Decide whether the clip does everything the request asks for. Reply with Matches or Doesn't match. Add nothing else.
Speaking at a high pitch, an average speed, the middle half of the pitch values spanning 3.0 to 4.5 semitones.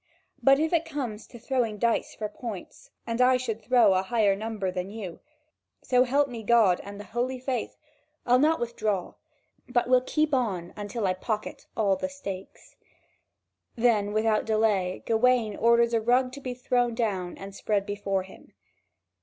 Matches